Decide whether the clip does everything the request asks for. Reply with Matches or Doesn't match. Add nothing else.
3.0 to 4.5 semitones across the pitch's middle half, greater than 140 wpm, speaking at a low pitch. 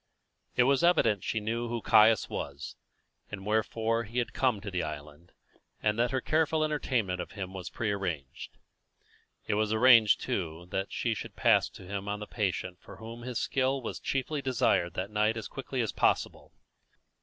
Matches